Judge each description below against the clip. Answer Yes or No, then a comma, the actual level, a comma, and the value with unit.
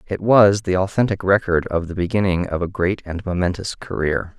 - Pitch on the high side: No, very low, 95 Hz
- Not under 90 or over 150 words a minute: No, average, 190 wpm